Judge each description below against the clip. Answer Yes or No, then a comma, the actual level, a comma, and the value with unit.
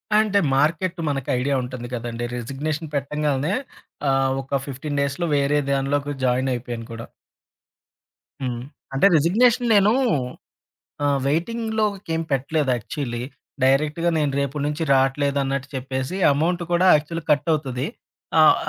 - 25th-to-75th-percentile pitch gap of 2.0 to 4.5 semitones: Yes, average, 3.5 semitones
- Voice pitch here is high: No, medium, 140 Hz